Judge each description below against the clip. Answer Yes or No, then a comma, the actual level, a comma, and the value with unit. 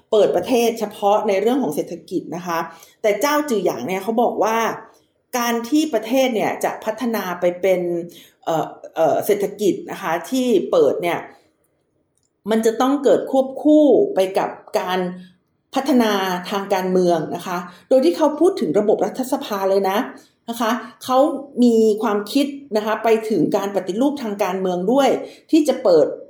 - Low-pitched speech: No, high, 220 Hz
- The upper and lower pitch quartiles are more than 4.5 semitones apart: Yes, wide, 5.5 semitones